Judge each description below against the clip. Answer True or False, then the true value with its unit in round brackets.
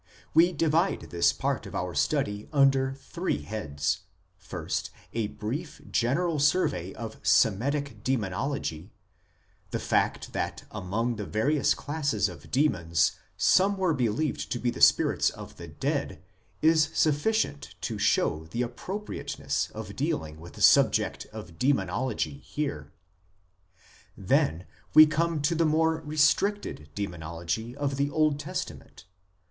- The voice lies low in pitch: True (130 Hz)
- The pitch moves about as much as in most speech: False (8.9 semitones)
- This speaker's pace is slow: True (130 wpm)